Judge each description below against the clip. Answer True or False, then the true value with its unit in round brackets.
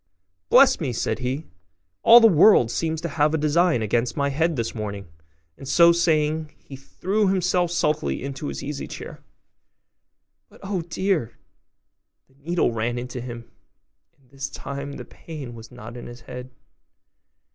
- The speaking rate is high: False (155 wpm)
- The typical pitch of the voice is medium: True (145 Hz)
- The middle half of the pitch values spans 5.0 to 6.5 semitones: True (5.3 semitones)